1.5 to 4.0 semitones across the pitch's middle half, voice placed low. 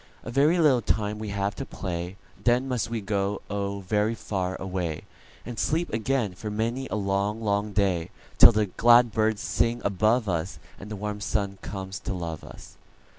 Yes: average, 2.8 semitones; low, 105 Hz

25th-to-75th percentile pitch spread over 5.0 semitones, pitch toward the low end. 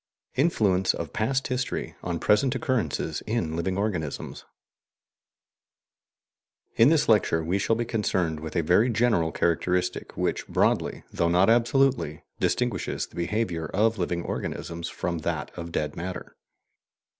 Yes: wide, 5.4 semitones; very low, 95 Hz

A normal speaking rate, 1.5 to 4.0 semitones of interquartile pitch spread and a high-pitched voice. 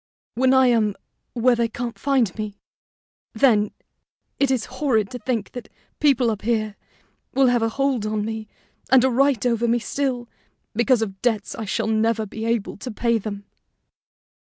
Yes: average, 170 wpm; average, 2.8 semitones; high, 235 Hz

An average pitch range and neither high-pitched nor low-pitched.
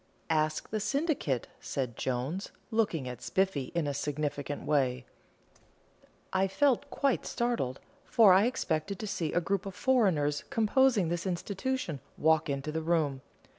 No: wide, 6.8 semitones; medium, 170 Hz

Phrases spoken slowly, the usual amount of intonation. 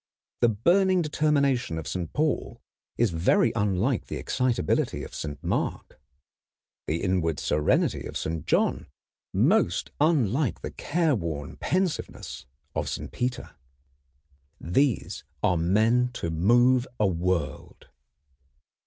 No: slow, 110 wpm; wide, 8.3 semitones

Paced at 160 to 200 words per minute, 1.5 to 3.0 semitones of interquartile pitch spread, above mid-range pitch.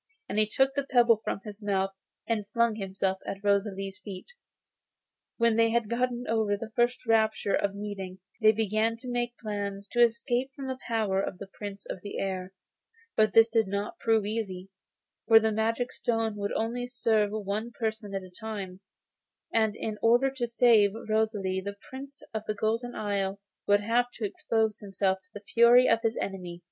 Yes: average, 180 wpm; narrow, 2.5 semitones; high, 220 Hz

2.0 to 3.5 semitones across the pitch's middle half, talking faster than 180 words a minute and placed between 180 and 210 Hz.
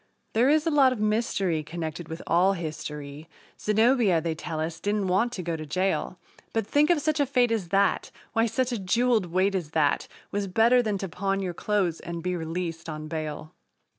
No: wide, 5.5 semitones; average, 200 wpm; high, 190 Hz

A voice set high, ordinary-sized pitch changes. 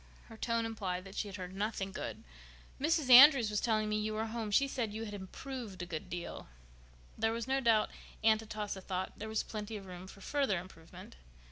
Yes: high, 215 Hz; average, 3.1 semitones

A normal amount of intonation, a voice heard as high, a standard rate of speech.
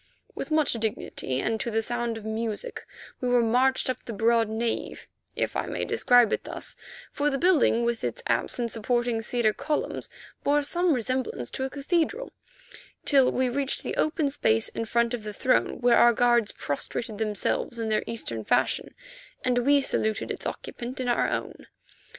Yes: average, 3.0 semitones; high, 240 Hz; average, 180 wpm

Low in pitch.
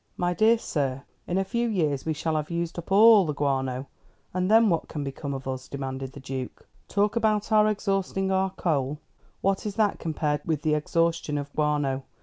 No: medium, 160 Hz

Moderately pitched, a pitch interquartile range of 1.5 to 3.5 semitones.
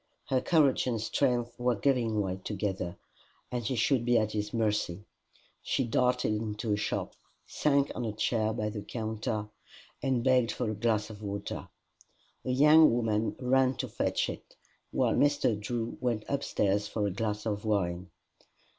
No: low, 110 Hz; average, 3.0 semitones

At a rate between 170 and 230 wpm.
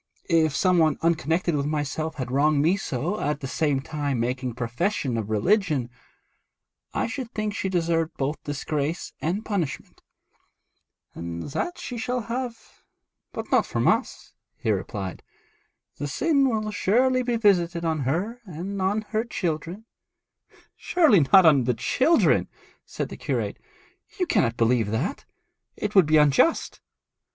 No: average, 145 wpm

